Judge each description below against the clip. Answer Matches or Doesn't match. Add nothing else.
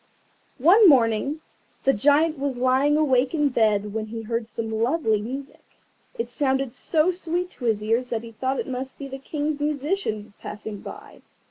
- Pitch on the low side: Doesn't match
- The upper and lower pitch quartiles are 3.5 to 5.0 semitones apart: Matches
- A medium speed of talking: Matches